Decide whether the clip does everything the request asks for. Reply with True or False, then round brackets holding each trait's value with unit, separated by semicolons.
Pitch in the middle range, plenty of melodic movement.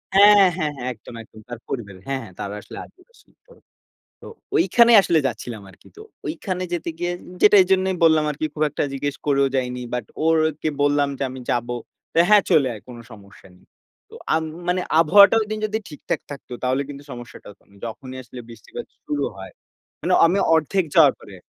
True (145 Hz; 6.6 semitones)